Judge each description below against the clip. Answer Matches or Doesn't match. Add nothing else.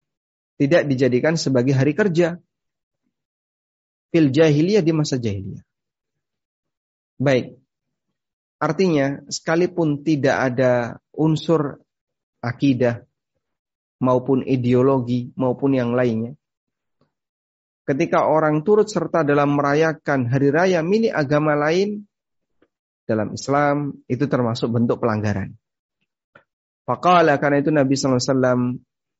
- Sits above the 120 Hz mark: Matches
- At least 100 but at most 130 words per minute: Doesn't match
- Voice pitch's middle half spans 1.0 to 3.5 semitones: Doesn't match